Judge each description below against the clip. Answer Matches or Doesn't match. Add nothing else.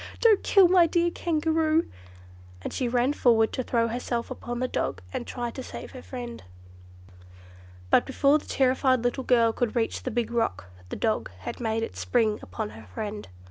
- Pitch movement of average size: Matches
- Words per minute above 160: Matches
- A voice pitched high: Matches